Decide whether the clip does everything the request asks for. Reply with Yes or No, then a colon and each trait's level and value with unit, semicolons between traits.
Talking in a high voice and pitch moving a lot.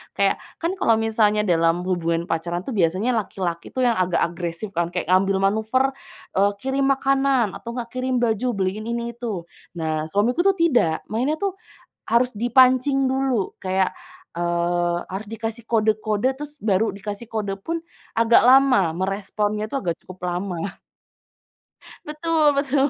Yes: high, 215 Hz; wide, 5.7 semitones